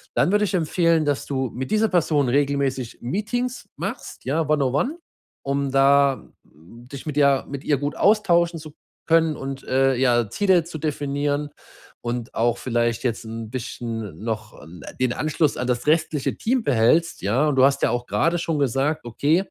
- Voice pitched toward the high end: No, medium, 140 Hz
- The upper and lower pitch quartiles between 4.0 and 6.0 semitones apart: Yes, average, 4.6 semitones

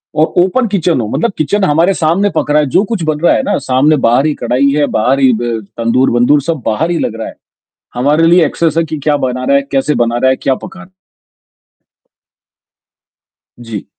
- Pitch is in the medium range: Yes, medium, 145 Hz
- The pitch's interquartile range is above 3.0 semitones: Yes, average, 4.7 semitones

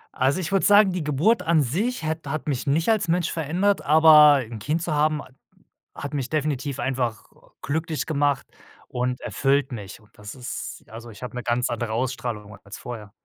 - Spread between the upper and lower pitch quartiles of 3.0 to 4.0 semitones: No, average, 4.7 semitones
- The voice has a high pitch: No, medium, 145 Hz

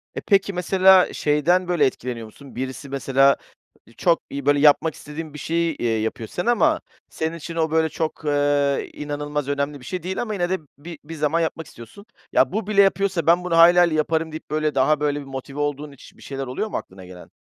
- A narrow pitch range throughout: No, average, 3.6 semitones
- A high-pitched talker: No, medium, 150 Hz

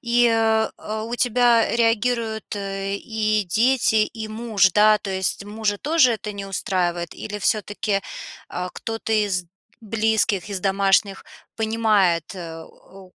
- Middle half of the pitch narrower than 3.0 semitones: Yes, narrow, 2.4 semitones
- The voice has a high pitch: Yes, high, 215 Hz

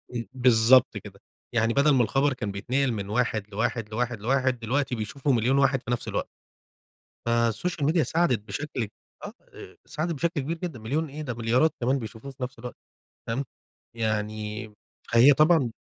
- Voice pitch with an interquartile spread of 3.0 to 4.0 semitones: Yes, average, 3.6 semitones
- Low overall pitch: Yes, low, 125 Hz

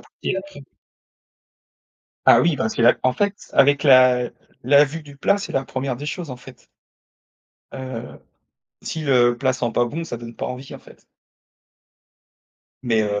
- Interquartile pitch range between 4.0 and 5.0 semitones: No, average, 3.2 semitones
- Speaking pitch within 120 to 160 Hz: Yes, low, 130 Hz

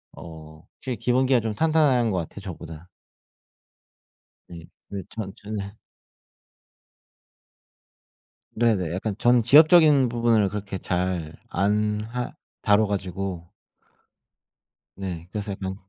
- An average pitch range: Yes, average, 4.6 semitones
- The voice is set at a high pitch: No, low, 105 Hz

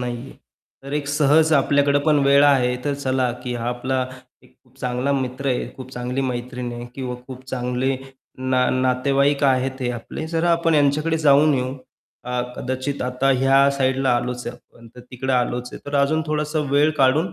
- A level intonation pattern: Yes, narrow, 2.2 semitones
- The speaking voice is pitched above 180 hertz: No, low, 130 Hz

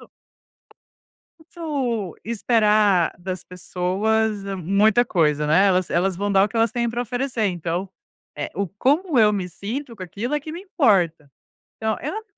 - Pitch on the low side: No, high, 210 Hz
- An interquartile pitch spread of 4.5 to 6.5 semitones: Yes, average, 4.8 semitones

